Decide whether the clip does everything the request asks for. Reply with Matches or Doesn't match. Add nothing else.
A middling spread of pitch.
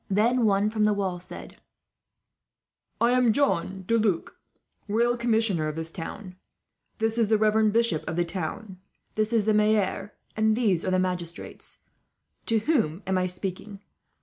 Matches